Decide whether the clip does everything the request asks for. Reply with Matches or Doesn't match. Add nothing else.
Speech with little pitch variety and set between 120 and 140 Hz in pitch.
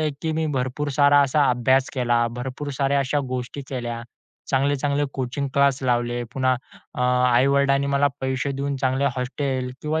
Matches